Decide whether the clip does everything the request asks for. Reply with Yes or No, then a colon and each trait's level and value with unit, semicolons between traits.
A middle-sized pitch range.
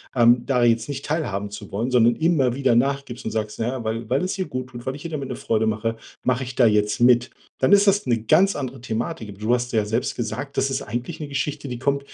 Yes: average, 3.4 semitones